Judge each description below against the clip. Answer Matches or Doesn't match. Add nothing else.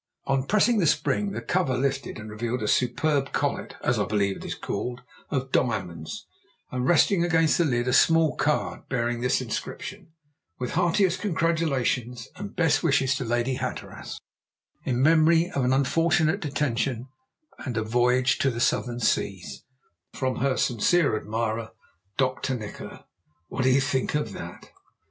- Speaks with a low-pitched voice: Matches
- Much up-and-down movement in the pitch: Doesn't match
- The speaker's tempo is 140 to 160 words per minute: Matches